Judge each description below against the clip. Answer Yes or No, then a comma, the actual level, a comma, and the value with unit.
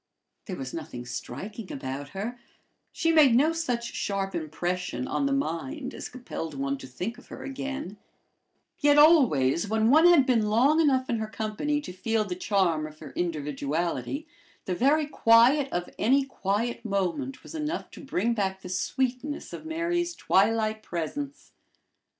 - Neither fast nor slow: Yes, average, 160 wpm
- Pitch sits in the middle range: No, high, 225 Hz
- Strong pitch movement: Yes, wide, 7.7 semitones